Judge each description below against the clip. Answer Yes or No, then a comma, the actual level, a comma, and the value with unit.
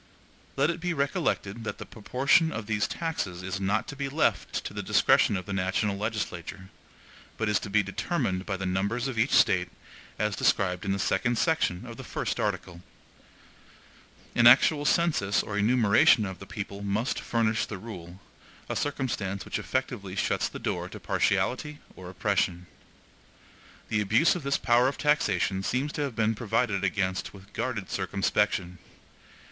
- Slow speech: No, average, 165 wpm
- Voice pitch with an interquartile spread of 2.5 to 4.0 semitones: No, average, 4.7 semitones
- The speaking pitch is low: Yes, low, 105 Hz